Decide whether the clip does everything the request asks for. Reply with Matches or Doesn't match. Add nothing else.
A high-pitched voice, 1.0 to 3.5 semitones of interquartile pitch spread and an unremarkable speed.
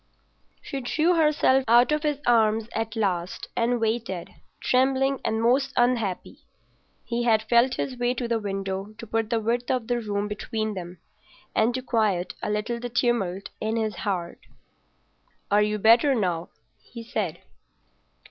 Matches